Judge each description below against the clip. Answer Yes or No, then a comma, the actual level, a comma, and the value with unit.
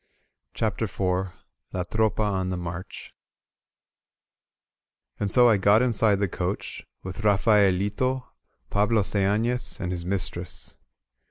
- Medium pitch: No, low, 100 Hz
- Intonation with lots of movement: No, average, 2.9 semitones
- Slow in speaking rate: Yes, slow, 110 wpm